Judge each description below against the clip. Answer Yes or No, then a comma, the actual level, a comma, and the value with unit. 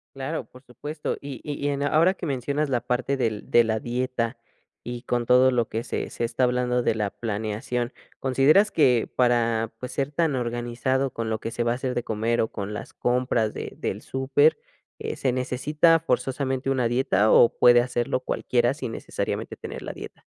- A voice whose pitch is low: Yes, low, 125 Hz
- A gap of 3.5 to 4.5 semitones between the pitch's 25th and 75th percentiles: No, narrow, 2.4 semitones